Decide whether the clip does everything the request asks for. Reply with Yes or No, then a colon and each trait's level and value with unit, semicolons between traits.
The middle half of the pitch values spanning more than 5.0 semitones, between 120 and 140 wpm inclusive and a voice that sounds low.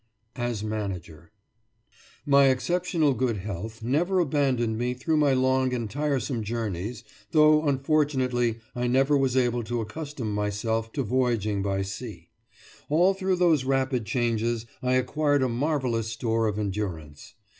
No: average, 4.2 semitones; slow, 135 wpm; low, 125 Hz